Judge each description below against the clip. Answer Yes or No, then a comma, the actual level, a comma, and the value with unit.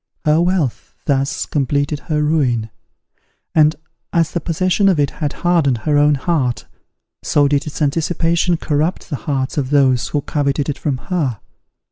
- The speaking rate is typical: Yes, average, 155 wpm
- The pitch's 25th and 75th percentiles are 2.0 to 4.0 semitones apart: Yes, average, 2.9 semitones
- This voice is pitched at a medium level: Yes, medium, 150 Hz